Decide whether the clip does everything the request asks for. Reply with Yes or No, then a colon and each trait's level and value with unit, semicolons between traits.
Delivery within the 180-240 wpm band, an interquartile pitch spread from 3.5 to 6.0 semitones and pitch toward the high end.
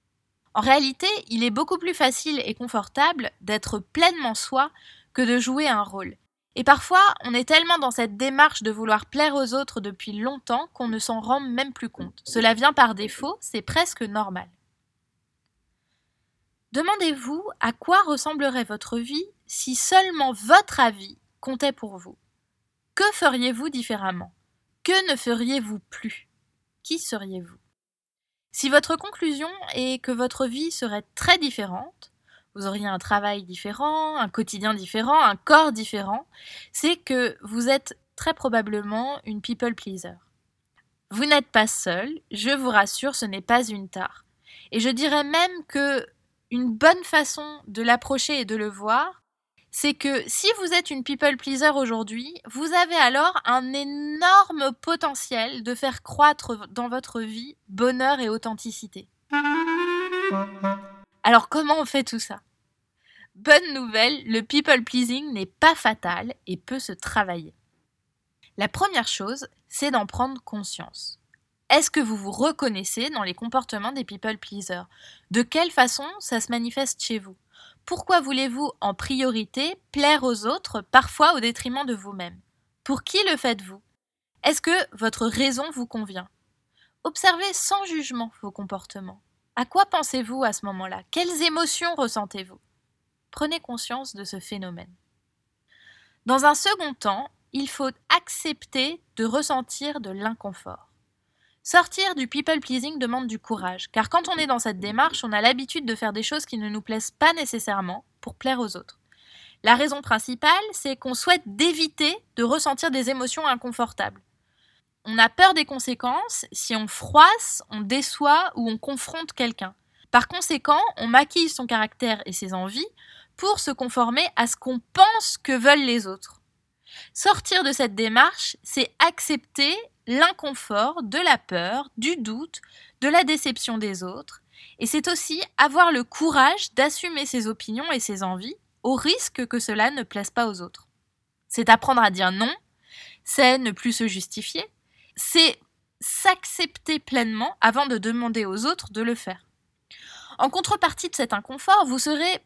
No: average, 155 wpm; wide, 5.5 semitones; very high, 255 Hz